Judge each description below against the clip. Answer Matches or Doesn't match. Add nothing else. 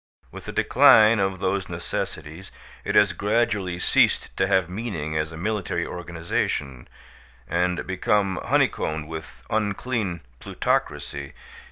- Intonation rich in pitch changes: Doesn't match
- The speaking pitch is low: Matches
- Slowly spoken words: Matches